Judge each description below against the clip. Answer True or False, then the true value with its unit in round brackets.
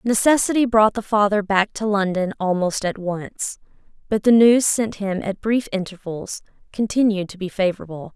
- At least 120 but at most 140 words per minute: False (160 wpm)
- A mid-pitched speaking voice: False (205 Hz)